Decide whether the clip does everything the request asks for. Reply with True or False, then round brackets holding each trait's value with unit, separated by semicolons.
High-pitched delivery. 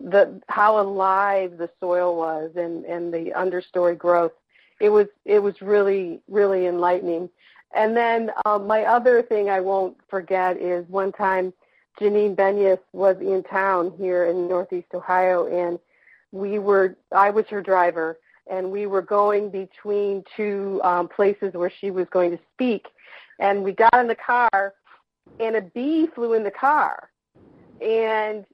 True (195 Hz)